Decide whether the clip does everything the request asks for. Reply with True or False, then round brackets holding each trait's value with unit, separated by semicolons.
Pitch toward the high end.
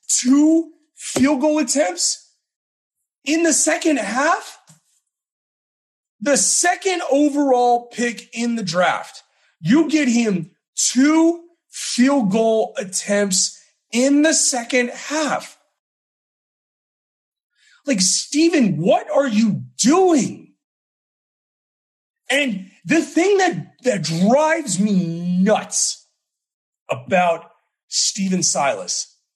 True (255 Hz)